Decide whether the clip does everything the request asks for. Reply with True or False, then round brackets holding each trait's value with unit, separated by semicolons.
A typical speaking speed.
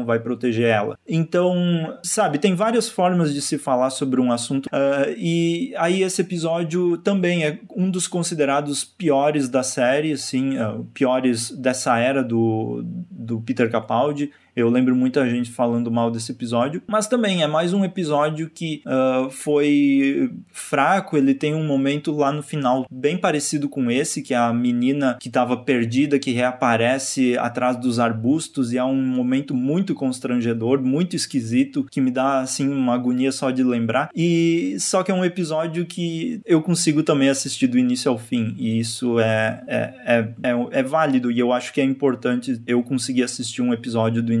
True (175 wpm)